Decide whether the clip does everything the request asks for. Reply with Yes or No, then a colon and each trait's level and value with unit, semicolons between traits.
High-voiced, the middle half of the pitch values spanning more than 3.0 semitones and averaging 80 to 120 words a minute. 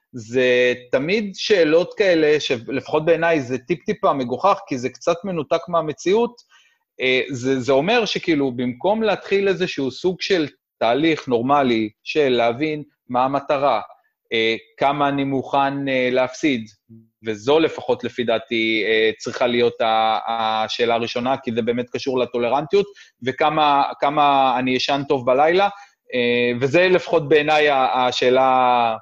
No: low, 135 Hz; average, 4.9 semitones; average, 115 wpm